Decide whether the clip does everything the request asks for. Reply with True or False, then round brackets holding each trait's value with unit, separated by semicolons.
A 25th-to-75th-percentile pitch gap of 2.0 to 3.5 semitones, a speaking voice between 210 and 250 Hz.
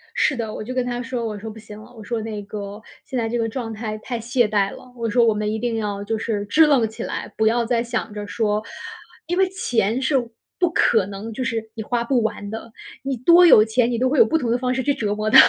True (2.7 semitones; 230 Hz)